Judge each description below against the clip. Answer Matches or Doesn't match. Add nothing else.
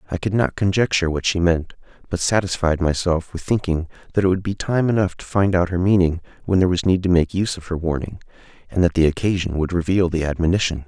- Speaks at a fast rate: Matches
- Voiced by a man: Matches